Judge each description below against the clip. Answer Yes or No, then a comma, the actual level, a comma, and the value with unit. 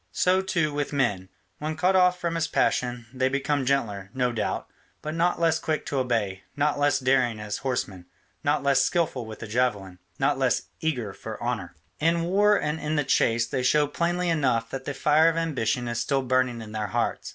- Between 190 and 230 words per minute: Yes, average, 200 wpm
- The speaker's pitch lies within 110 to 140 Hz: Yes, low, 135 Hz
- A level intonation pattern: No, average, 5.1 semitones